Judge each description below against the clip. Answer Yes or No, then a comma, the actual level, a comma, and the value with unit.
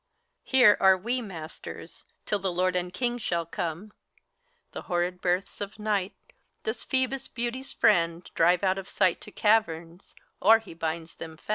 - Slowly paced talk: No, average, 160 wpm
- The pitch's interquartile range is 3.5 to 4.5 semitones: Yes, average, 4.1 semitones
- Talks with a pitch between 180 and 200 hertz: Yes, high, 190 Hz